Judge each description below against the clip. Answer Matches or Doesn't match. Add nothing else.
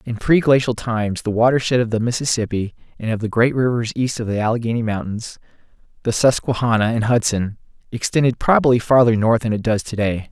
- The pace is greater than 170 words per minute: Matches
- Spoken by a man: Matches